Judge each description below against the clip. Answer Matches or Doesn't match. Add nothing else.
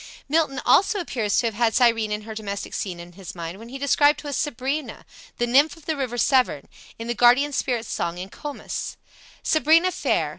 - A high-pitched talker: Matches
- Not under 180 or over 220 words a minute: Matches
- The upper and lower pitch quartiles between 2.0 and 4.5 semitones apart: Doesn't match